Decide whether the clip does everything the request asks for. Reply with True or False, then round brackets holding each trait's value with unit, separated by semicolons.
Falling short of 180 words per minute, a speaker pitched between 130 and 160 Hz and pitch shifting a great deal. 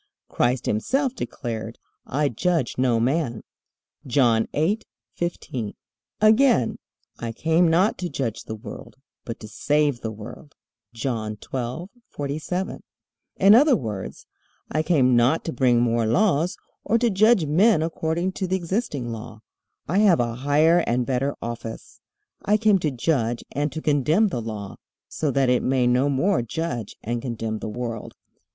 True (145 wpm; 140 Hz; 6.7 semitones)